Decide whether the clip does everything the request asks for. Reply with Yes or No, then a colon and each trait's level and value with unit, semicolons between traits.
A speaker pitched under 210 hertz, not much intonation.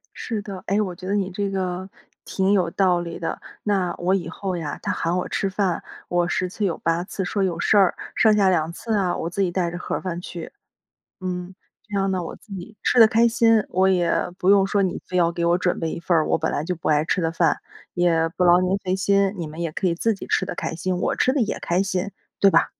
Yes: medium, 185 Hz; narrow, 2.3 semitones